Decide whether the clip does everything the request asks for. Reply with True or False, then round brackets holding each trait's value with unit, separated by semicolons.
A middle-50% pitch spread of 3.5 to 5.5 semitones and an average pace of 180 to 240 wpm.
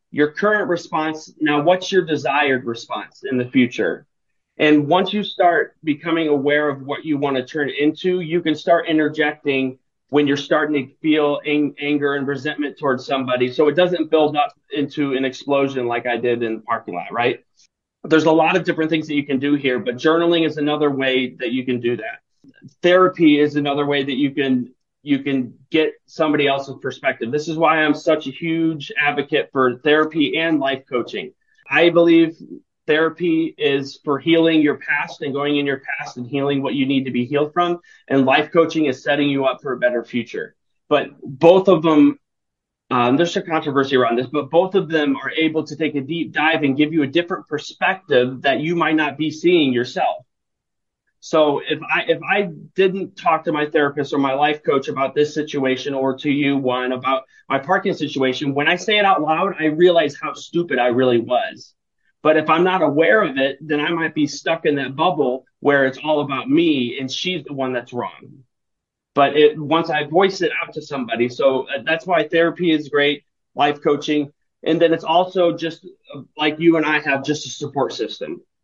False (3.0 semitones; 200 wpm)